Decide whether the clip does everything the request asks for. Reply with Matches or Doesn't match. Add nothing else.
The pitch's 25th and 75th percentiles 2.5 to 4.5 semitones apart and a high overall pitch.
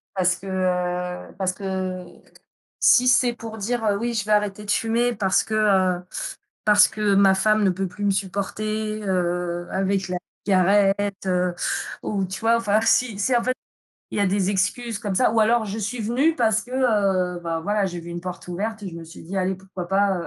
Matches